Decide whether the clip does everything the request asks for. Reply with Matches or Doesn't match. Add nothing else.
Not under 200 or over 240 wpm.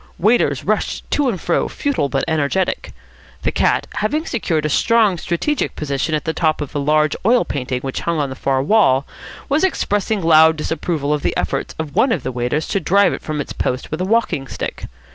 Matches